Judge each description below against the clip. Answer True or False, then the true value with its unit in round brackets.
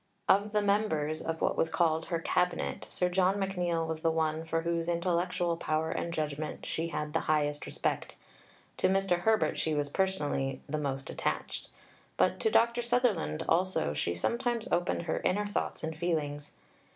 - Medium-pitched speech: True (170 Hz)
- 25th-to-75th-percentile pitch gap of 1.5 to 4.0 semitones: True (3.5 semitones)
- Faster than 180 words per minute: False (170 wpm)